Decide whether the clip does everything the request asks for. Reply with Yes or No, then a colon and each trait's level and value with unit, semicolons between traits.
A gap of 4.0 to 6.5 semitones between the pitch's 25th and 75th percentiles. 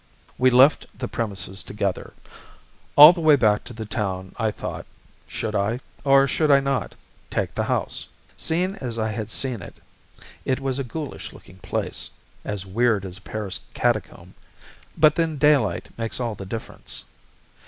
Yes: average, 5.0 semitones